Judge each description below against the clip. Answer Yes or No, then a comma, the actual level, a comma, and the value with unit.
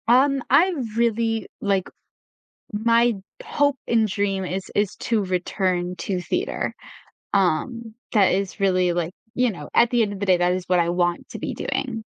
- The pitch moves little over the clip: No, average, 4.3 semitones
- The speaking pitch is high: Yes, high, 200 Hz